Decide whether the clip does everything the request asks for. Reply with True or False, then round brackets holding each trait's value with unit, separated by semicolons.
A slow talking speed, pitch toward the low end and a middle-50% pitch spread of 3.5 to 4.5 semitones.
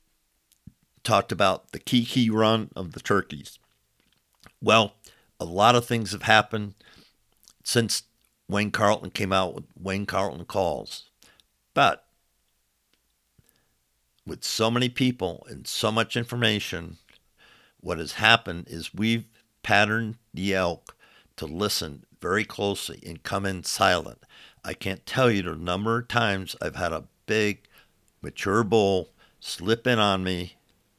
True (130 wpm; 100 Hz; 4.1 semitones)